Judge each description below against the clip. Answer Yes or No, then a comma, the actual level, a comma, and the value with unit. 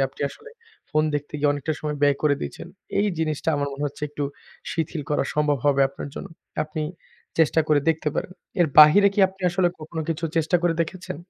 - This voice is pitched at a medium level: Yes, medium, 155 Hz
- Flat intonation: Yes, narrow, 2.2 semitones